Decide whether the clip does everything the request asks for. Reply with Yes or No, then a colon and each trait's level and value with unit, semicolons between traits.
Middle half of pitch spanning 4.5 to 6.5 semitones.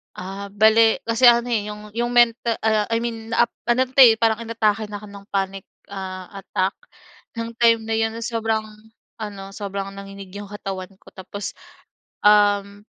No: narrow, 2.4 semitones